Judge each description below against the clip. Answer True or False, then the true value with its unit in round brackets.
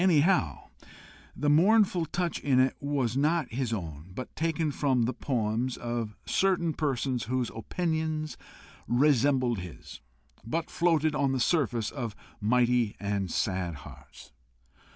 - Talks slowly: True (130 wpm)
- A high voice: False (130 Hz)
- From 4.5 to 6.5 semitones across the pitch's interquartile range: True (5.6 semitones)